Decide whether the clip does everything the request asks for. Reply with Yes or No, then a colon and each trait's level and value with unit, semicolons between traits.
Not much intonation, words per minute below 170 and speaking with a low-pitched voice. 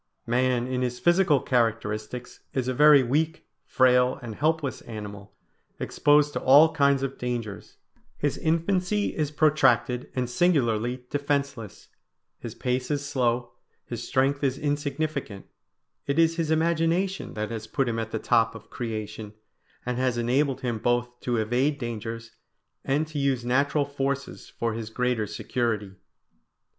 No: average, 3.7 semitones; average, 145 wpm; low, 130 Hz